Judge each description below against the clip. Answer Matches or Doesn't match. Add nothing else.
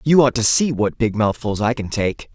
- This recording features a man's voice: Matches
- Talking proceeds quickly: Matches